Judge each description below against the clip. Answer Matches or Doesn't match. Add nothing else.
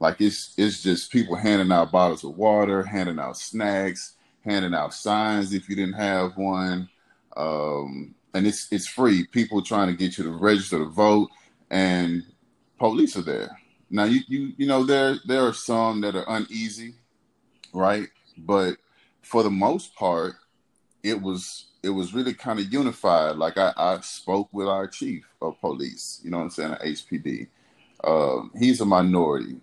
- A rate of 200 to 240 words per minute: Doesn't match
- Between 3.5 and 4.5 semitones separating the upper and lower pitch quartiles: Doesn't match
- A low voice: Matches